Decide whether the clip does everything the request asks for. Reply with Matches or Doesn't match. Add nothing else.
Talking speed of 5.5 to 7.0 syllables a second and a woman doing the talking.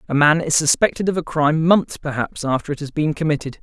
Doesn't match